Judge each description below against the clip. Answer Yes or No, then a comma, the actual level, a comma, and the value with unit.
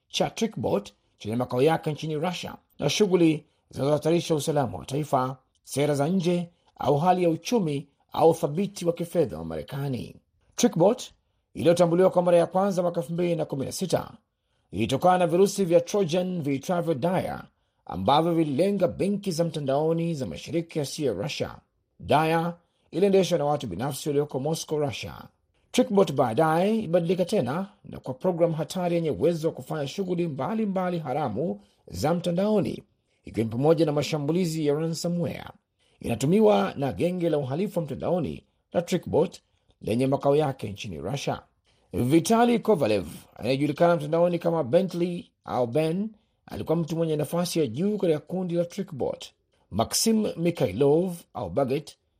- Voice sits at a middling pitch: Yes, medium, 165 Hz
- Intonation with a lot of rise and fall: No, average, 3.9 semitones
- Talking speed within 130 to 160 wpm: Yes, average, 135 wpm